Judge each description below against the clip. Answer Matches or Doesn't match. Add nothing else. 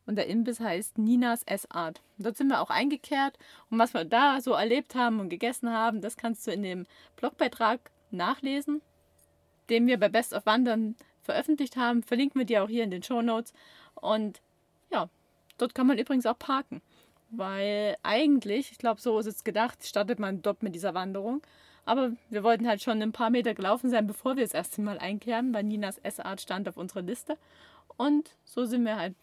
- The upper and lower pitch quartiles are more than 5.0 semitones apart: Doesn't match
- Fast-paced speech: Matches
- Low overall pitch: Doesn't match